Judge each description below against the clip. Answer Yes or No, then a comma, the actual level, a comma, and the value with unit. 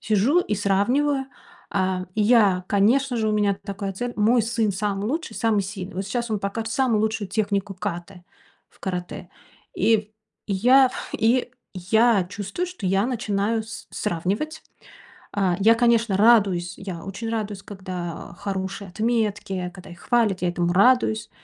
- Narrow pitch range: No, average, 3.2 semitones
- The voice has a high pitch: Yes, high, 205 Hz